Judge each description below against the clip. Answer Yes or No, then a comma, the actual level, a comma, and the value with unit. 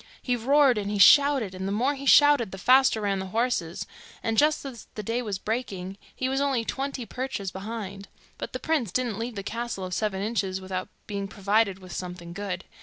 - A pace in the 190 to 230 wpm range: Yes, fast, 205 wpm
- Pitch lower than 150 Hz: No, high, 215 Hz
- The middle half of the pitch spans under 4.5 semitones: No, average, 4.8 semitones